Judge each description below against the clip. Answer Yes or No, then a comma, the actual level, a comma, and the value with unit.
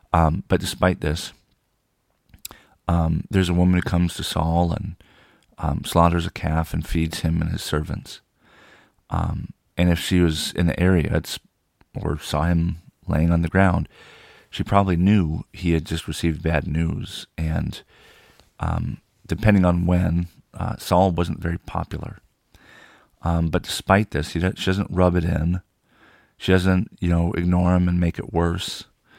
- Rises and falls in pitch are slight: Yes, narrow, 2.0 semitones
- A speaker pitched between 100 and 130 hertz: No, very low, 85 Hz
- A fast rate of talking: No, average, 160 wpm